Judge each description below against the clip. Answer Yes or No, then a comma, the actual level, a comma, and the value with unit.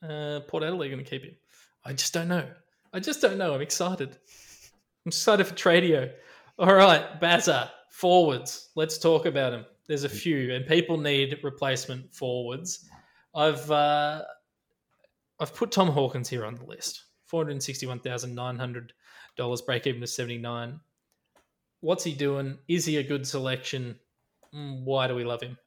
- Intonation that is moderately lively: Yes, average, 4.6 semitones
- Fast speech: No, average, 170 wpm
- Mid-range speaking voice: Yes, medium, 145 Hz